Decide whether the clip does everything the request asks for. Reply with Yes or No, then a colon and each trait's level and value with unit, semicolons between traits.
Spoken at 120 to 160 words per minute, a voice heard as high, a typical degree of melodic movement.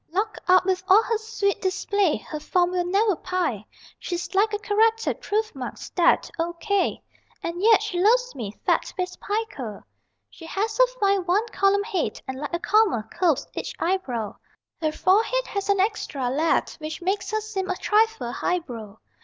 No: average, 170 wpm; very high, 380 Hz; average, 4.1 semitones